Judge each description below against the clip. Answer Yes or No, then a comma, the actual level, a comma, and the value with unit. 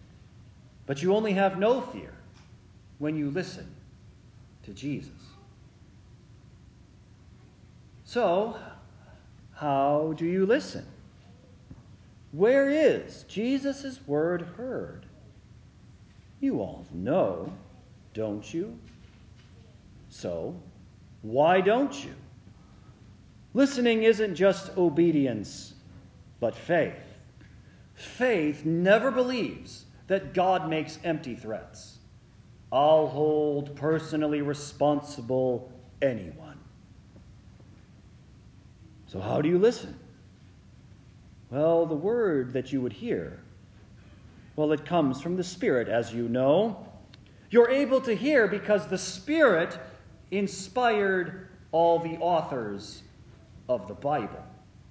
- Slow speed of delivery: Yes, slow, 90 wpm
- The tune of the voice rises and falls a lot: Yes, wide, 8.5 semitones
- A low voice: Yes, low, 130 Hz